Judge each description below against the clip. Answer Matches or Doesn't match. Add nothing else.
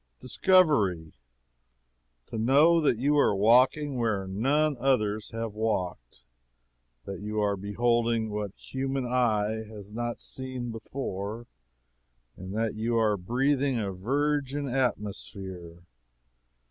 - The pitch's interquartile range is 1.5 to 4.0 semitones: Doesn't match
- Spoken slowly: Matches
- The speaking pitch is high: Doesn't match